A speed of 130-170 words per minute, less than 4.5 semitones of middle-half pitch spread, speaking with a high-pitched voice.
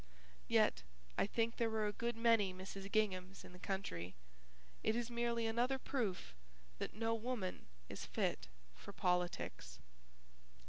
Yes: average, 140 wpm; average, 4.0 semitones; high, 215 Hz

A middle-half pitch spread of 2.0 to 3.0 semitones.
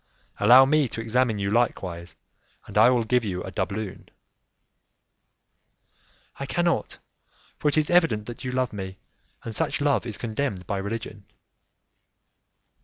No: average, 4.4 semitones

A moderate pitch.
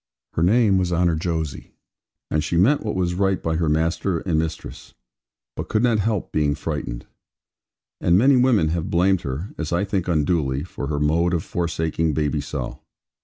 No: very low, 85 Hz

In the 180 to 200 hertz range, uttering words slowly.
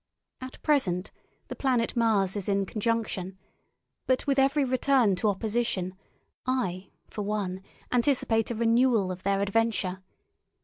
No: high, 220 Hz; slow, 130 wpm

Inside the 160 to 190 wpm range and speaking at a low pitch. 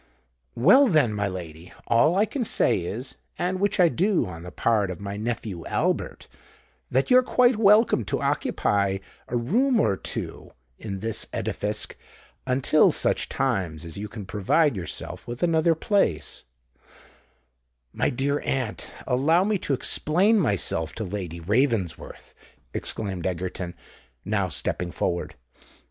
No: slow, 135 wpm; low, 115 Hz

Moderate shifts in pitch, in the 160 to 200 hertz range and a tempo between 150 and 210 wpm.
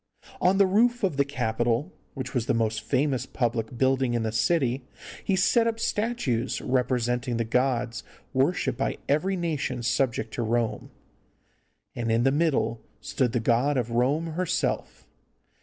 No: average, 4.6 semitones; low, 130 Hz; average, 155 wpm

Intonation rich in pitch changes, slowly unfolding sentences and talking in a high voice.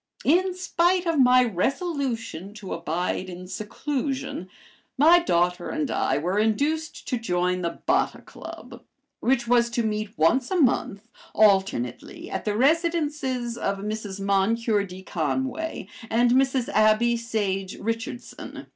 Yes: wide, 5.7 semitones; slow, 130 wpm; high, 230 Hz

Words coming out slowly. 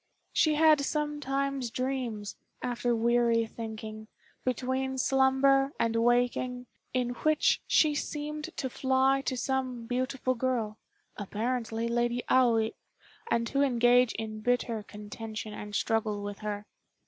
Yes: slow, 120 wpm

